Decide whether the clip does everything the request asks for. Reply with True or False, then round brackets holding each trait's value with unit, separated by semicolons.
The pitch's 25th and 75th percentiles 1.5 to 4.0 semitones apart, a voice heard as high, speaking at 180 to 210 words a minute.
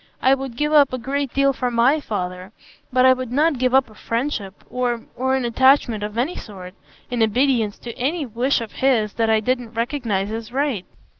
True (3.3 semitones; 245 Hz; 200 wpm)